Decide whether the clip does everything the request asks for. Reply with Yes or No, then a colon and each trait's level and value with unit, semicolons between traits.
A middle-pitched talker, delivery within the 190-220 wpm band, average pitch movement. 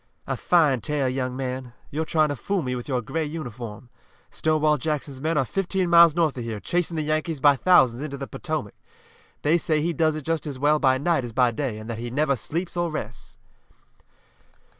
Yes: medium, 150 Hz; fast, 205 wpm; average, 3.9 semitones